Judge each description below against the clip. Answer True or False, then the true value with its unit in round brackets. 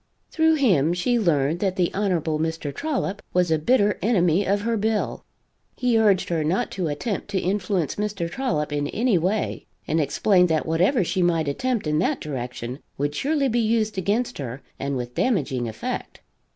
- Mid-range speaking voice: True (180 Hz)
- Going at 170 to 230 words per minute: True (180 wpm)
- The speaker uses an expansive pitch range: True (6.1 semitones)